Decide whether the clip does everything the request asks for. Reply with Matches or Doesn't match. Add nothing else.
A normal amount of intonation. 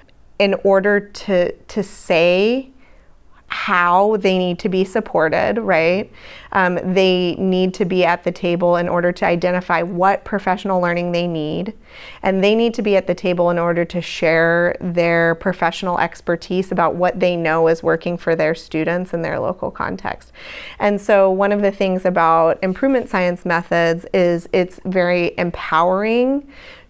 Doesn't match